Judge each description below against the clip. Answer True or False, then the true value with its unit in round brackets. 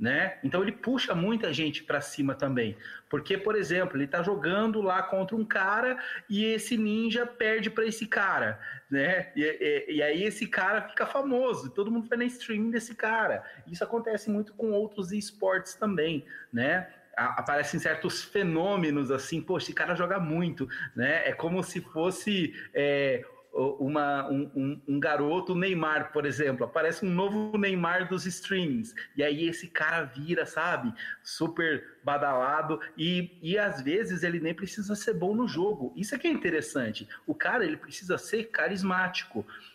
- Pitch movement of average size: False (5.7 semitones)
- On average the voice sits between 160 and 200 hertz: True (185 Hz)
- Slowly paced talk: False (165 wpm)